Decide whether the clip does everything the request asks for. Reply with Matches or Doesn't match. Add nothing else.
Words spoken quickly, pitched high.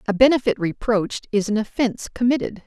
Doesn't match